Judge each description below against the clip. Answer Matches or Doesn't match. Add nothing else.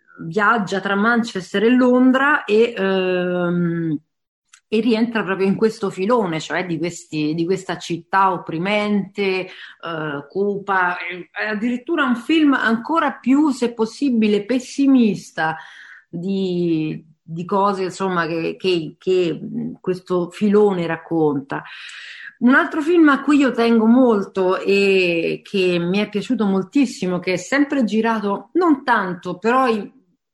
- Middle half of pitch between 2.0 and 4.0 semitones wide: Doesn't match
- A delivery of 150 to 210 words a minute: Doesn't match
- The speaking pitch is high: Matches